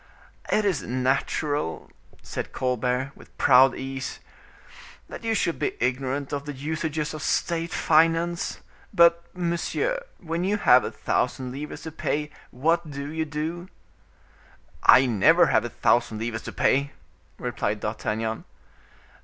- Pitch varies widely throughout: No, average, 4.4 semitones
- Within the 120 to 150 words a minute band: Yes, slow, 135 wpm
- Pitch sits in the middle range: Yes, medium, 145 Hz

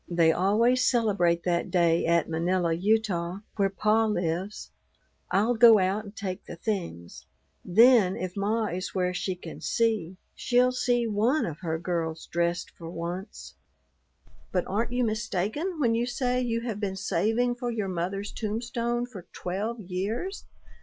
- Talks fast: No, average, 155 wpm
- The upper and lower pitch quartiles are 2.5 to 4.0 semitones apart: No, average, 4.7 semitones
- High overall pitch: Yes, high, 200 Hz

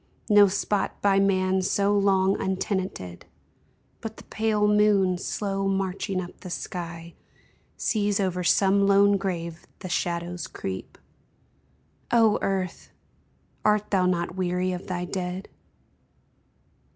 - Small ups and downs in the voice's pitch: Yes, narrow, 1.9 semitones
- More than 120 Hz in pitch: Yes, high, 190 Hz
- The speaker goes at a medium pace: No, slow, 115 wpm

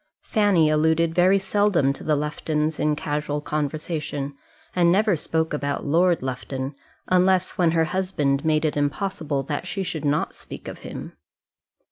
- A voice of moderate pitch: Yes, medium, 155 Hz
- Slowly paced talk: No, average, 150 wpm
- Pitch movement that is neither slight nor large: Yes, average, 3.5 semitones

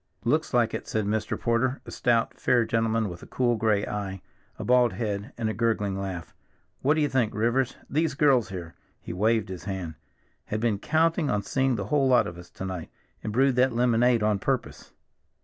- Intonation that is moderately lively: Yes, average, 3.8 semitones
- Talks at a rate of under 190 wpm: No, average, 195 wpm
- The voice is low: Yes, low, 115 Hz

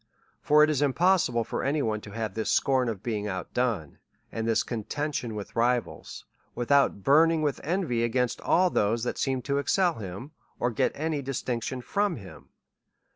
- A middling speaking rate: Yes, average, 180 wpm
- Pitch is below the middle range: Yes, low, 125 Hz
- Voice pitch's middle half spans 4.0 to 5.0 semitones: Yes, average, 4.7 semitones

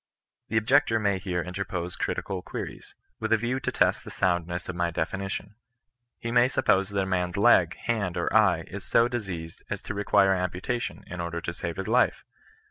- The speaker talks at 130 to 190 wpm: No, average, 200 wpm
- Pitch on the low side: Yes, very low, 95 Hz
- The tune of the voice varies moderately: Yes, average, 3.6 semitones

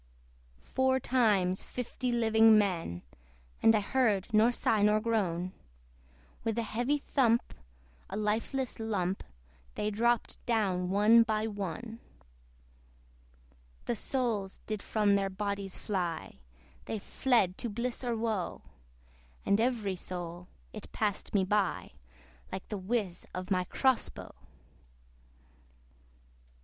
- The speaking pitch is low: No, high, 215 Hz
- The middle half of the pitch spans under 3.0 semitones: No, average, 3.3 semitones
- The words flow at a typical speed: No, slow, 115 wpm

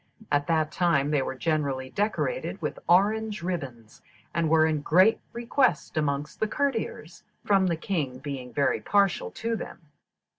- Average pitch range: No, wide, 6.0 semitones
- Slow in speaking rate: No, average, 150 wpm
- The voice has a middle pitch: Yes, medium, 165 Hz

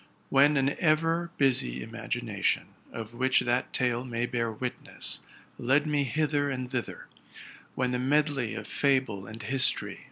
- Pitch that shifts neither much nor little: Yes, average, 3.1 semitones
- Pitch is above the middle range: No, low, 130 Hz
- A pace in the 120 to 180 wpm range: Yes, average, 150 wpm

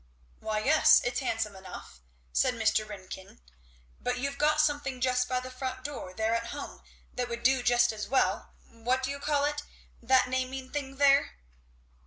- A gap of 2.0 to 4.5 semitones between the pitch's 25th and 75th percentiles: Yes, average, 3.3 semitones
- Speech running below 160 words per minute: No, average, 175 wpm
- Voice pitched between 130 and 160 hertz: No, very high, 255 Hz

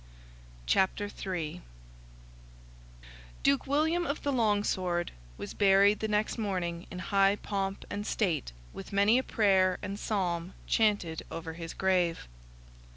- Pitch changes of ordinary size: Yes, average, 3.3 semitones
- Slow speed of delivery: Yes, slow, 130 wpm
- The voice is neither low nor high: No, high, 195 Hz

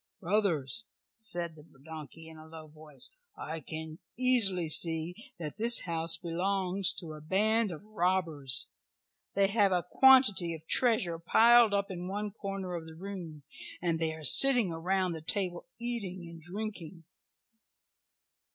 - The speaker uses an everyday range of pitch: Yes, average, 4.0 semitones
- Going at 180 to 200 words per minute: No, average, 145 wpm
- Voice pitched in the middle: Yes, medium, 180 Hz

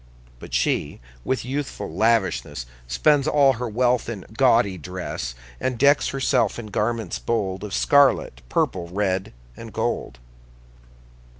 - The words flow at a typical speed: No, slow, 125 wpm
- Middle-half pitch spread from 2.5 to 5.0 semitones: No, wide, 5.6 semitones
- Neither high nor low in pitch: No, low, 115 Hz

